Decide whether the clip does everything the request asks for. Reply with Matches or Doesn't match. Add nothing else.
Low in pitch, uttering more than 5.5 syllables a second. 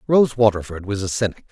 Matches